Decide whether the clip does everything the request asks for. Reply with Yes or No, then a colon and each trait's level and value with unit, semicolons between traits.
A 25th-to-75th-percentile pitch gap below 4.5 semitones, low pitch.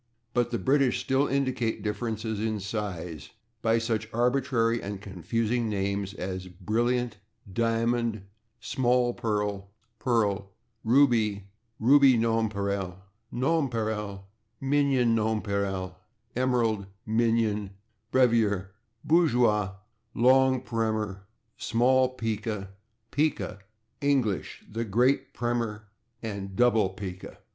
Yes: average, 3.3 semitones; low, 115 Hz